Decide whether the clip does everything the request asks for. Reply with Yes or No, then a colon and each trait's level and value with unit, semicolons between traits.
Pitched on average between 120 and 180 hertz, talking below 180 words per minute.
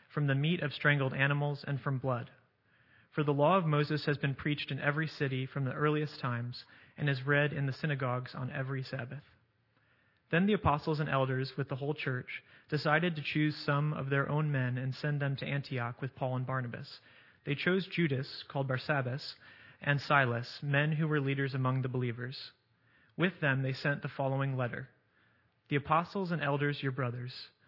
No: medium, 140 Hz; average, 185 wpm